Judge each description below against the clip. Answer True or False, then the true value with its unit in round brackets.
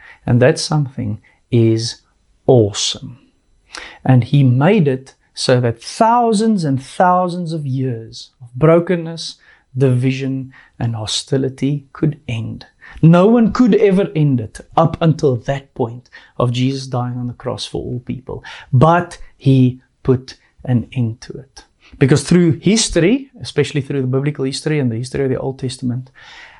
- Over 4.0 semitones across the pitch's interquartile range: True (4.4 semitones)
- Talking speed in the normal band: True (145 wpm)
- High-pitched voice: False (135 Hz)